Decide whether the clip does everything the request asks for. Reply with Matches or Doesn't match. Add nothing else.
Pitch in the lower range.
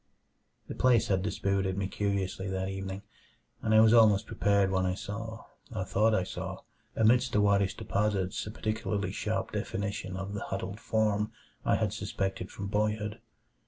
Matches